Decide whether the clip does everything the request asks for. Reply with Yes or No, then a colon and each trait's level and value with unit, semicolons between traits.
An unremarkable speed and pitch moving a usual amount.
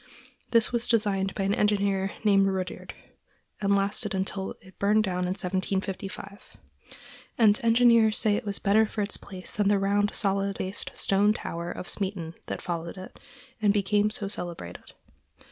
No: average, 160 wpm; narrow, 1.6 semitones